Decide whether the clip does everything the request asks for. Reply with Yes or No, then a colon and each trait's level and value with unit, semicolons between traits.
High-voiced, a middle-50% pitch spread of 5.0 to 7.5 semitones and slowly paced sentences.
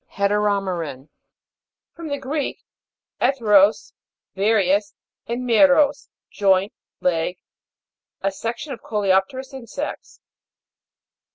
Yes: high, 210 Hz; wide, 5.4 semitones; slow, 80 wpm